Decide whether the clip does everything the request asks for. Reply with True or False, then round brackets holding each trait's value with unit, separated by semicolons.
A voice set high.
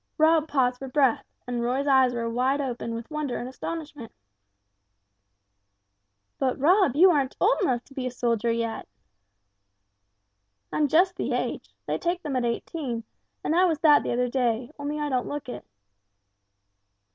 True (265 Hz)